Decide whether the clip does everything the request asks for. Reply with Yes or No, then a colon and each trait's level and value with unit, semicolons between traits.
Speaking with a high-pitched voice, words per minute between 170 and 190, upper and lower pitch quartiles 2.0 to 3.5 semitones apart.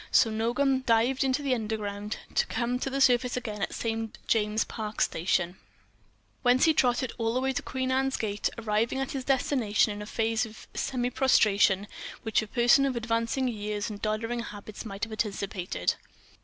Yes: high, 230 Hz; average, 180 wpm; average, 3.2 semitones